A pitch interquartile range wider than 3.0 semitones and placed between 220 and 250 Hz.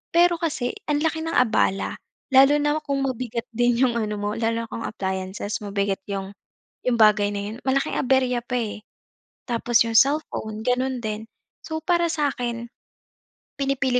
Yes: average, 4.1 semitones; high, 240 Hz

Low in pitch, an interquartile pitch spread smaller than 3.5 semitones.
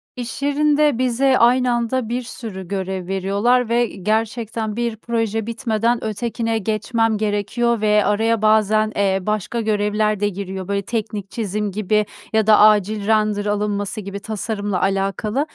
No: high, 215 Hz; narrow, 2.4 semitones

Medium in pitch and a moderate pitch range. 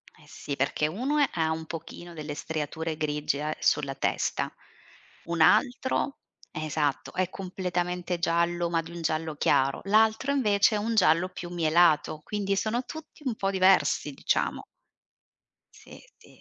Yes: medium, 175 Hz; average, 4.4 semitones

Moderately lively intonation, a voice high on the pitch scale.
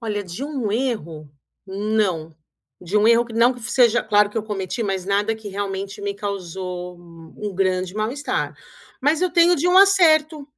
Yes: average, 4.4 semitones; high, 210 Hz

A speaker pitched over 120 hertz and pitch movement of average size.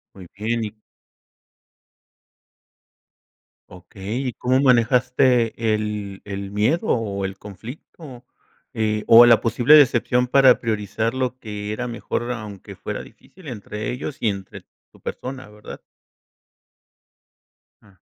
No: low, 115 Hz; average, 3.2 semitones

